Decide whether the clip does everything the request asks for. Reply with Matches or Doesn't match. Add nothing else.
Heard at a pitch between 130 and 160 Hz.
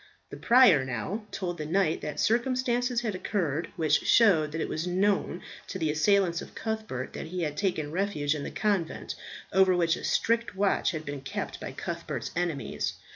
Doesn't match